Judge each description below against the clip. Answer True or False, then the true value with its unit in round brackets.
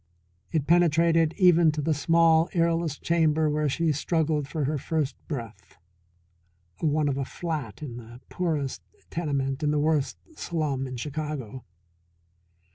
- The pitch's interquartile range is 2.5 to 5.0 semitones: True (3.0 semitones)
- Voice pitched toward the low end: False (155 Hz)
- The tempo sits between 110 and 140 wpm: True (135 wpm)